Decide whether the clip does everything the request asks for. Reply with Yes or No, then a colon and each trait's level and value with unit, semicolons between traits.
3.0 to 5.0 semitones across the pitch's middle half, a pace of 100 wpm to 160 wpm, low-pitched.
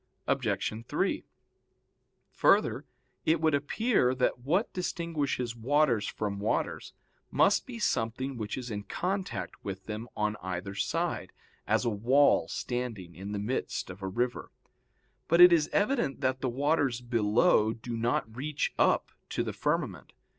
No: wide, 5.6 semitones; average, 145 wpm; low, 125 Hz